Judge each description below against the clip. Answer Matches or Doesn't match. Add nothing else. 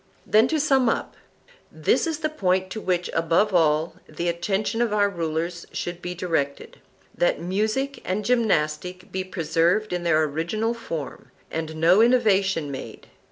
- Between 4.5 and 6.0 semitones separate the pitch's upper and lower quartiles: Matches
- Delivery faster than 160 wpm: Doesn't match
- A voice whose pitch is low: Doesn't match